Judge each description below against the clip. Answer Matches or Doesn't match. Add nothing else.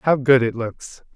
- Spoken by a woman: Doesn't match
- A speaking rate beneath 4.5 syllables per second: Matches